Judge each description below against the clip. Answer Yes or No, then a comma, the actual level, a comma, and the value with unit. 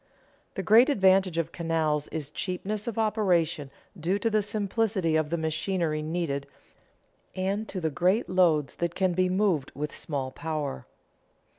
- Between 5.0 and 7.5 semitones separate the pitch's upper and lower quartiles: No, average, 4.0 semitones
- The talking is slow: No, average, 150 wpm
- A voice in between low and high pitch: Yes, medium, 175 Hz